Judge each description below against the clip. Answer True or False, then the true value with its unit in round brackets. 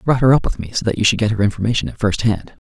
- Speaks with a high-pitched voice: False (110 Hz)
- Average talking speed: False (360 wpm)